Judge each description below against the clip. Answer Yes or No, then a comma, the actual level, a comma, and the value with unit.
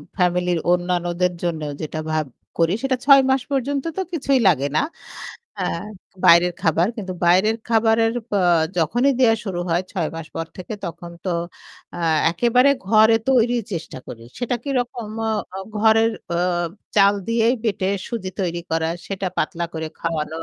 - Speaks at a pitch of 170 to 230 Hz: Yes, high, 190 Hz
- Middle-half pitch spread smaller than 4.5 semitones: No, average, 5.2 semitones